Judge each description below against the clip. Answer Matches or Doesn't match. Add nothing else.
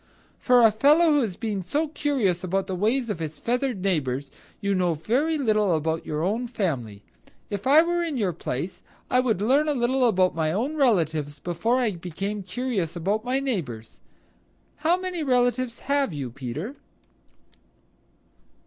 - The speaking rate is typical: Matches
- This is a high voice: Matches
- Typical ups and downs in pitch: Doesn't match